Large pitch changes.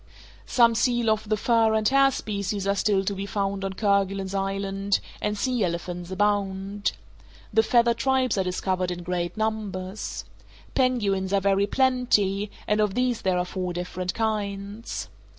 No: narrow, 2.5 semitones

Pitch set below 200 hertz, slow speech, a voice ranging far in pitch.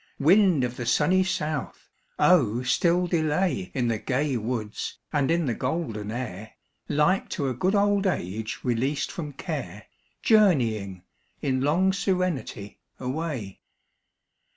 Yes: medium, 140 Hz; slow, 130 wpm; wide, 7.1 semitones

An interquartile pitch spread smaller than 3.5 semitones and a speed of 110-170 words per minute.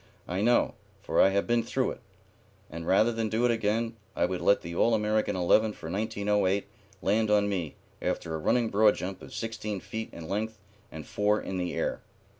No: average, 2.9 semitones; average, 200 wpm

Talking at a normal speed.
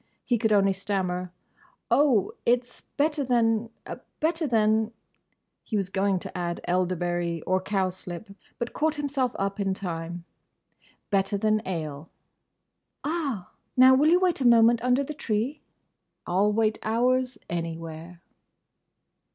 No: slow, 120 wpm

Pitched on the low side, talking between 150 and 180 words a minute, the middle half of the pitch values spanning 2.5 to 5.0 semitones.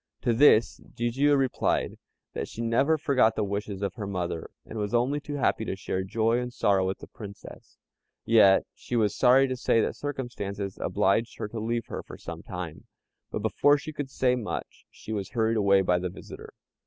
No: low, 115 Hz; average, 195 wpm; average, 4.0 semitones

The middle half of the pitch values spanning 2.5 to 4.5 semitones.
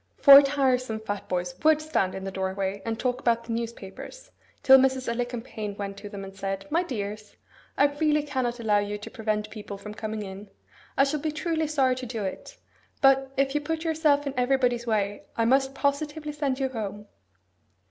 No: average, 5.2 semitones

